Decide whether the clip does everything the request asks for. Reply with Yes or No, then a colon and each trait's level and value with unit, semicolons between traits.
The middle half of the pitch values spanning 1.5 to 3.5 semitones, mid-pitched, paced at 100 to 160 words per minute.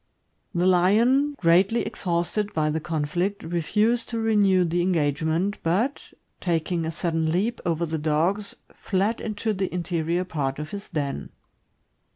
No: average, 4.0 semitones; medium, 175 Hz; average, 140 wpm